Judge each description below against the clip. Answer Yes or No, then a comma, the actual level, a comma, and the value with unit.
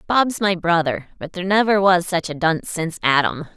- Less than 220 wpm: Yes, average, 200 wpm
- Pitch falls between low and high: Yes, medium, 175 Hz